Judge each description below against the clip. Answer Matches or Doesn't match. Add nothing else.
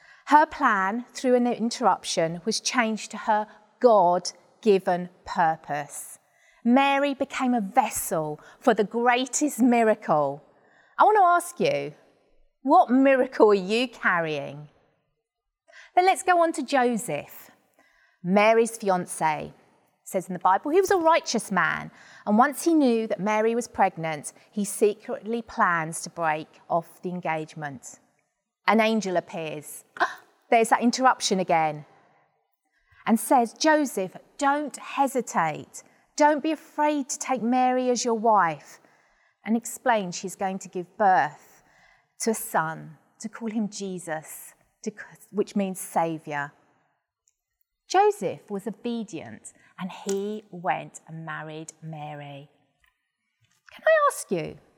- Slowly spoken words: Matches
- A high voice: Matches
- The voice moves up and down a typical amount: Doesn't match